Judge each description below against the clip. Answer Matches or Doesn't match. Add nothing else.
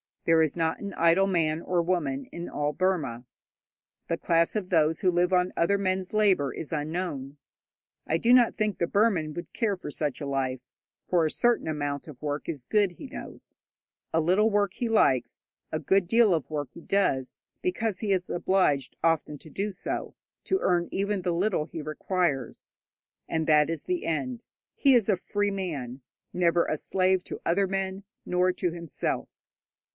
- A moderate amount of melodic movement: Matches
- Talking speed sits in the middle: Matches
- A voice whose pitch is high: Doesn't match